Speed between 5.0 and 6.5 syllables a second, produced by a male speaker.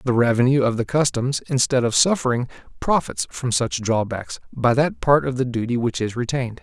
Yes: 5.4 syllables/s; male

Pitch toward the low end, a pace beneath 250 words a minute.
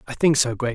No: low, 130 Hz; fast, 320 wpm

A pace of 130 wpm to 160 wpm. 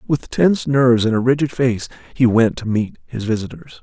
No: fast, 205 wpm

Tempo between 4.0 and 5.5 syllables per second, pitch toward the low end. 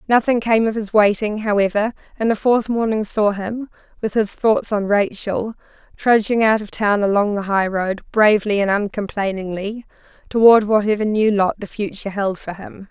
No: 5.0 syllables/s; high, 210 Hz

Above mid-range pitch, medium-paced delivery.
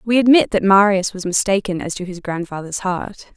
Yes: high, 195 Hz; average, 195 wpm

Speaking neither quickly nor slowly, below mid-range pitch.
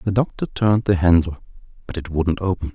Yes: average, 195 wpm; very low, 95 Hz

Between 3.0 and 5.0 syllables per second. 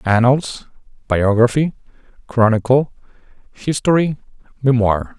Yes: 4.1 syllables/s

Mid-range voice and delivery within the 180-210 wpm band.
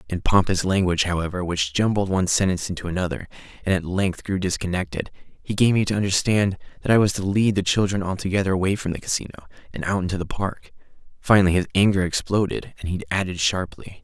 No: very low, 95 Hz; average, 190 wpm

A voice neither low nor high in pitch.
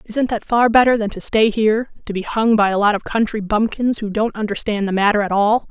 No: high, 215 Hz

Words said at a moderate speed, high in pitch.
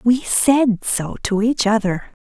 Yes: average, 160 wpm; high, 220 Hz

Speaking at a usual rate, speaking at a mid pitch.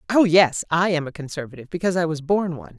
No: fast, 215 wpm; medium, 165 Hz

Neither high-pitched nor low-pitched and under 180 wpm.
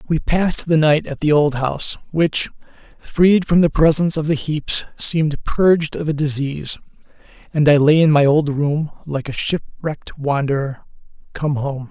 Yes: medium, 150 Hz; average, 170 wpm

